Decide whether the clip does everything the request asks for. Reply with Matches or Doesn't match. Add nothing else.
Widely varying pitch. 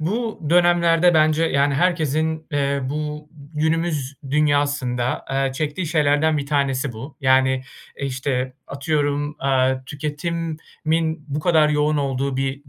Doesn't match